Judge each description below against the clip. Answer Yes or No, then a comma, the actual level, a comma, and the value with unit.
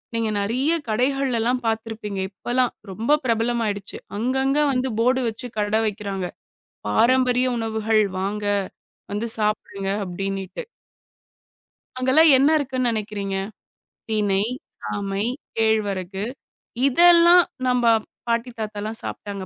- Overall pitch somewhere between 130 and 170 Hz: No, high, 225 Hz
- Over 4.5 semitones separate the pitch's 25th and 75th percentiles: No, average, 3.7 semitones